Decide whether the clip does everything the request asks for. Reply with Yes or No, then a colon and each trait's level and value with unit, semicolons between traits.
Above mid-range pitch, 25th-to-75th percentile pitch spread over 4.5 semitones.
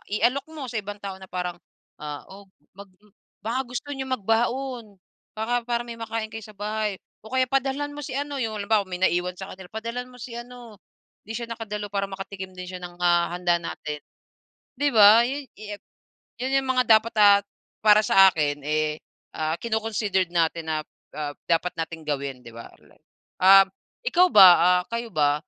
Yes: high, 210 Hz; average, 4.9 semitones